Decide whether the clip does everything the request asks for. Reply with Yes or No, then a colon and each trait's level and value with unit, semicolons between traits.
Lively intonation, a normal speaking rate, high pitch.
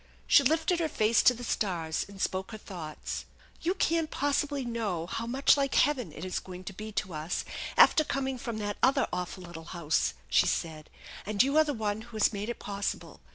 No: wide, 6.8 semitones; fast, 220 wpm; high, 215 Hz